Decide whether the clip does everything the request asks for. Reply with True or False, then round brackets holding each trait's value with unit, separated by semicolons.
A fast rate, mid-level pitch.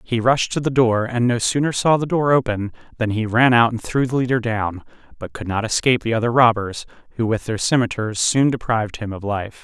False (230 wpm; 115 Hz)